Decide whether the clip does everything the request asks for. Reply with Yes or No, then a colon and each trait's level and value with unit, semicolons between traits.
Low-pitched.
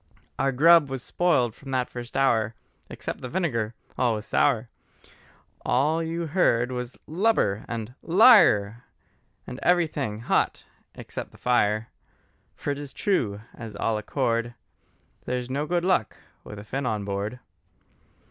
Yes: low, 125 Hz